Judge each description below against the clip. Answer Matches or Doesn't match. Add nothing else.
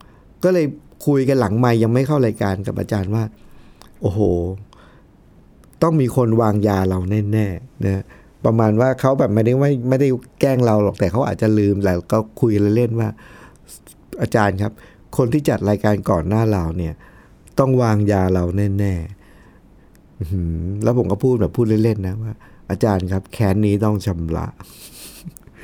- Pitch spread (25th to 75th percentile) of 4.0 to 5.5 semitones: Doesn't match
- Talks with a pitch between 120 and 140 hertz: Doesn't match